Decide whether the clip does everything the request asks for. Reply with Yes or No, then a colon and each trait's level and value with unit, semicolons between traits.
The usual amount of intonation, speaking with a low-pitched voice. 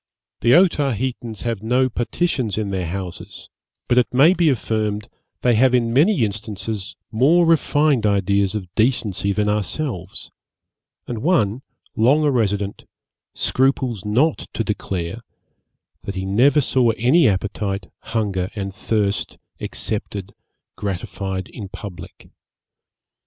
Yes: average, 4.5 semitones; low, 110 Hz